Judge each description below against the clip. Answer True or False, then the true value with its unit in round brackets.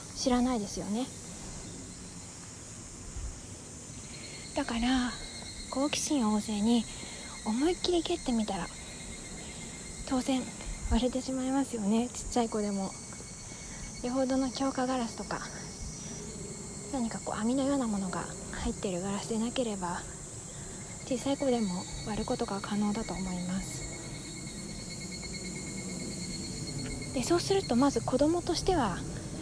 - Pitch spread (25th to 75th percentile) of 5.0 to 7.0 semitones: True (5.5 semitones)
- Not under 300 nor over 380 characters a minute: False (235 characters per minute)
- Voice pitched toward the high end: True (230 Hz)